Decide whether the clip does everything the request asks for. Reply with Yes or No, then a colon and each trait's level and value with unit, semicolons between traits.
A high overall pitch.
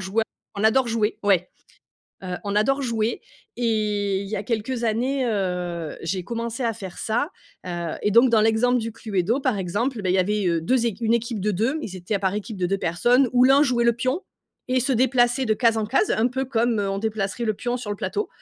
Yes: high, 220 Hz